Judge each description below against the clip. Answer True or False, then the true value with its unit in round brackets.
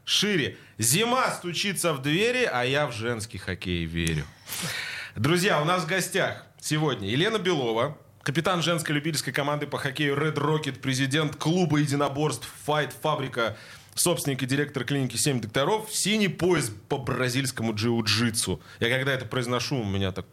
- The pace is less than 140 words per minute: False (150 wpm)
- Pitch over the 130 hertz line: True (140 Hz)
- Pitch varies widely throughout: False (4.6 semitones)